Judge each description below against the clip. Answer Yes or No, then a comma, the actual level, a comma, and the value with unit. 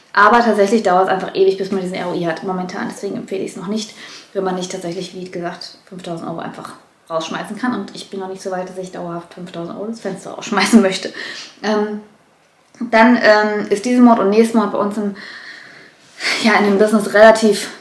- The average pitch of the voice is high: Yes, high, 200 Hz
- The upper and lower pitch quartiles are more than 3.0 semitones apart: No, average, 2.7 semitones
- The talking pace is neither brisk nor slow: No, fast, 210 wpm